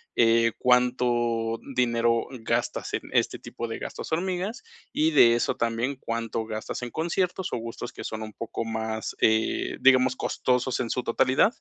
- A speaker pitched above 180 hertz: No, low, 120 Hz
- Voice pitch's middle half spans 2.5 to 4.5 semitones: No, narrow, 2.1 semitones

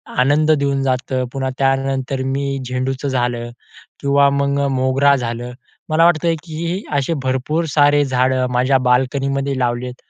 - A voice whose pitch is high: No, low, 135 Hz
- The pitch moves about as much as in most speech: No, narrow, 1.7 semitones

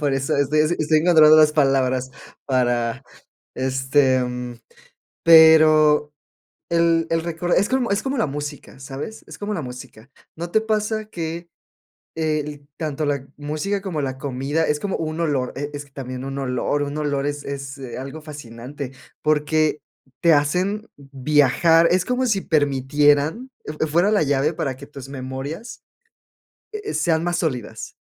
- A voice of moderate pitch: Yes, medium, 150 Hz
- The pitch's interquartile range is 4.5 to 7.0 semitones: No, average, 3.3 semitones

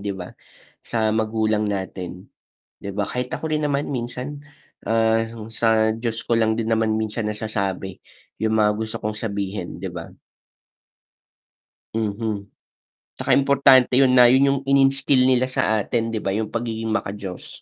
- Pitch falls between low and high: No, low, 110 Hz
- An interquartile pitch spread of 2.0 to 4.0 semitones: Yes, average, 2.8 semitones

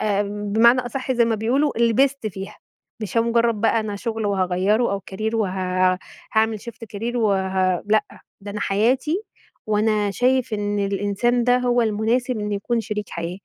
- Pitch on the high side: Yes, high, 215 Hz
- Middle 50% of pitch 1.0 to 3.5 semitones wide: Yes, average, 2.8 semitones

